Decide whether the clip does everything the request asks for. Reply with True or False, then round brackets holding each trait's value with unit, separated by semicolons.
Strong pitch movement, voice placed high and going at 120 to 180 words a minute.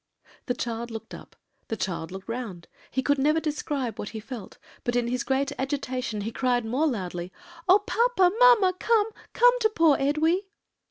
True (6.2 semitones; 265 Hz; 175 wpm)